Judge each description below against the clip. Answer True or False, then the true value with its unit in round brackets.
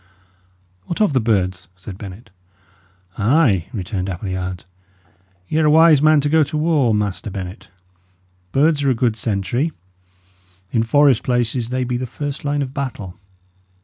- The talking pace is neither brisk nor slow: True (150 wpm)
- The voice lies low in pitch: True (120 Hz)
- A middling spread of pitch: False (6.5 semitones)